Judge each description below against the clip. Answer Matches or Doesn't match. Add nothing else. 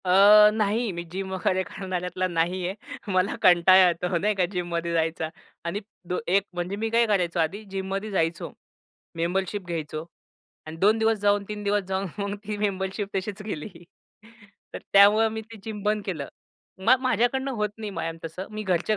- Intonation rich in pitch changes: Doesn't match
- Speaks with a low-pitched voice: Doesn't match